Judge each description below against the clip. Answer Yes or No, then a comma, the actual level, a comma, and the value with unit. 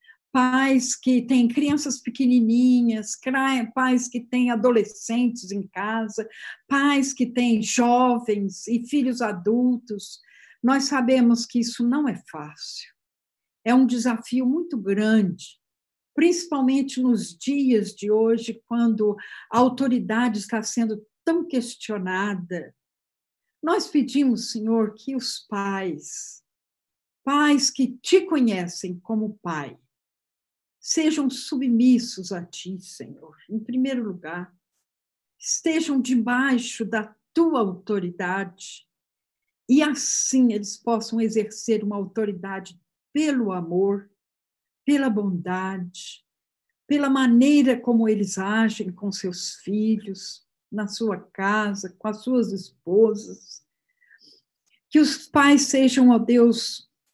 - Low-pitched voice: No, high, 230 Hz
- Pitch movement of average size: Yes, average, 4.2 semitones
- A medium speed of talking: No, slow, 105 wpm